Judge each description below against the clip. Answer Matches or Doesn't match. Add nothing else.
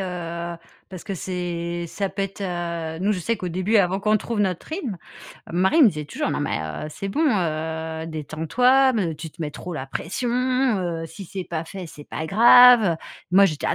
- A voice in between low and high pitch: Matches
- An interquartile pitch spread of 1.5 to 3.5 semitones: Doesn't match